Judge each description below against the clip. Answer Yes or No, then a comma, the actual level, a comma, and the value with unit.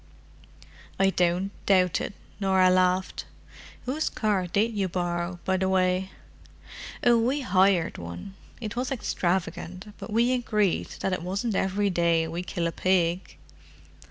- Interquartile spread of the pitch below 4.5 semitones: Yes, narrow, 2.6 semitones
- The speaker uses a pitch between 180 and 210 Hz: Yes, high, 190 Hz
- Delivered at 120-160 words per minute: Yes, average, 140 wpm